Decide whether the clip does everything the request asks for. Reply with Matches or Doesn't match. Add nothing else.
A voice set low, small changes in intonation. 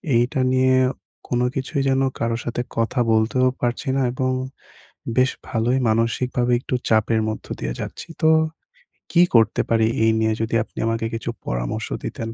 Matches